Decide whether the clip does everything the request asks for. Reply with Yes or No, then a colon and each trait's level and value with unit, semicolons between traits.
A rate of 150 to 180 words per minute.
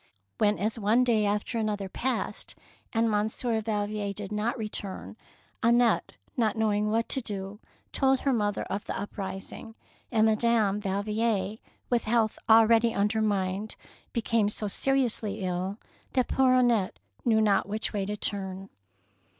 No: average, 140 wpm